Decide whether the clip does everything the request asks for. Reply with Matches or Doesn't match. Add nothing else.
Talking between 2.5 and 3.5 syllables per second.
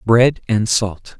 Matches